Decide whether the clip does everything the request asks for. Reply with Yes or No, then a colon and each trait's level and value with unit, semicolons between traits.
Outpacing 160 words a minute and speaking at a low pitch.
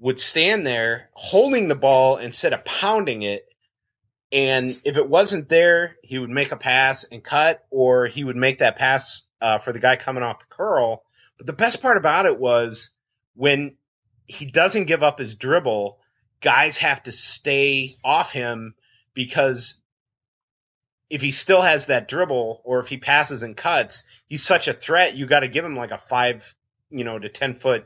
Yes: average, 185 wpm; low, 130 Hz